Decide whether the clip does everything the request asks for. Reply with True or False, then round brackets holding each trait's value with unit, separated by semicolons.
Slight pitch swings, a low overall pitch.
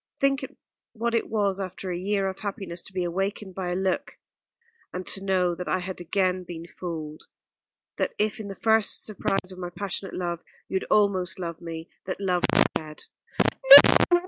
False (2.0 semitones; 185 Hz)